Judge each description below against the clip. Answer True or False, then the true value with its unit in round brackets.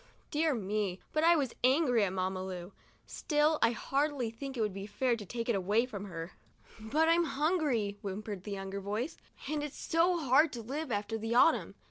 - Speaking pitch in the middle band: False (235 Hz)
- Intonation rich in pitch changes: True (6.6 semitones)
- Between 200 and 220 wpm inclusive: True (205 wpm)